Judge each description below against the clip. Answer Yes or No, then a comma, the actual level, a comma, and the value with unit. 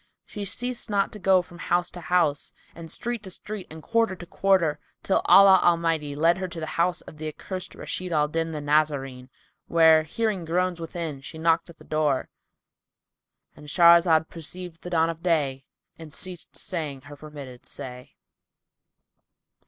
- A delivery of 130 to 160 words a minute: No, average, 170 wpm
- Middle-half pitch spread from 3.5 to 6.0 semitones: No, average, 3.0 semitones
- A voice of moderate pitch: Yes, medium, 165 Hz